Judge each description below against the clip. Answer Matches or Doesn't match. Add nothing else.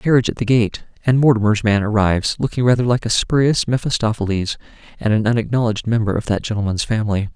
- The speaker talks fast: Doesn't match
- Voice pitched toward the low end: Matches